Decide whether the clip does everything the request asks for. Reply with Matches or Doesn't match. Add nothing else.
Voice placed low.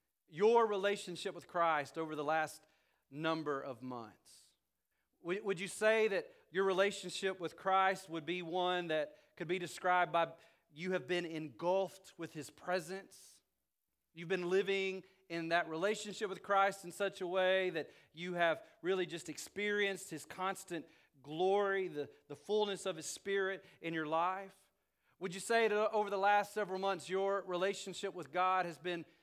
Doesn't match